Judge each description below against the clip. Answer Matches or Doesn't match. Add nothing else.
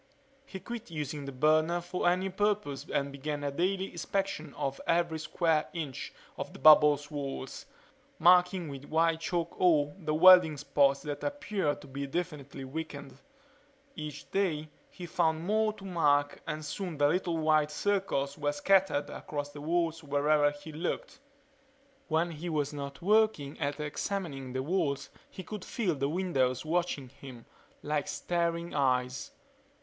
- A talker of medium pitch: Matches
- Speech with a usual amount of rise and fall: Matches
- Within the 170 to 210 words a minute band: Doesn't match